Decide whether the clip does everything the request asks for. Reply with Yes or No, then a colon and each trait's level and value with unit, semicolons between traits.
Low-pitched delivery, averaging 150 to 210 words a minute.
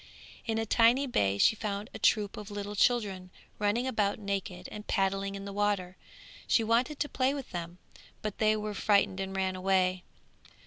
No: high, 205 Hz; average, 180 wpm